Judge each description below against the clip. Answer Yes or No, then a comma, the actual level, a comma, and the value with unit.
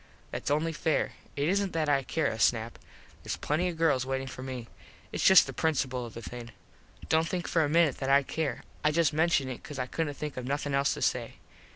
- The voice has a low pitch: No, medium, 145 Hz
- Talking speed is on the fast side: Yes, fast, 230 wpm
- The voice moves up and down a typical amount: Yes, average, 3.7 semitones